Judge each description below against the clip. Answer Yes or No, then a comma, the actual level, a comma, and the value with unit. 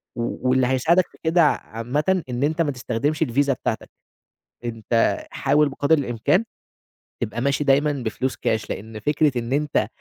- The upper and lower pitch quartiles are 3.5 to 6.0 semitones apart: Yes, average, 3.8 semitones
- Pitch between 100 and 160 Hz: Yes, low, 135 Hz